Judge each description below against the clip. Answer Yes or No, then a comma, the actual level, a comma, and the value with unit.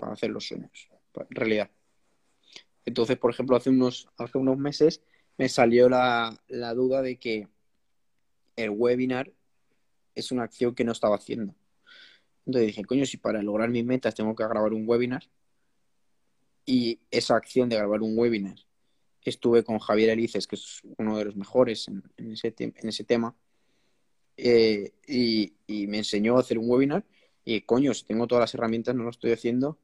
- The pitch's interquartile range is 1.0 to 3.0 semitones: Yes, narrow, 2.5 semitones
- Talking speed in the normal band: Yes, average, 175 wpm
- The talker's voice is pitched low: Yes, low, 115 Hz